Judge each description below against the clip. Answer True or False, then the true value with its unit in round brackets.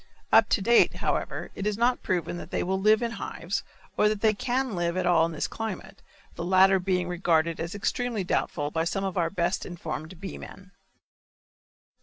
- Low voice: False (185 Hz)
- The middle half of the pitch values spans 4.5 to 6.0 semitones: False (3.5 semitones)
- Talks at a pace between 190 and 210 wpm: True (195 wpm)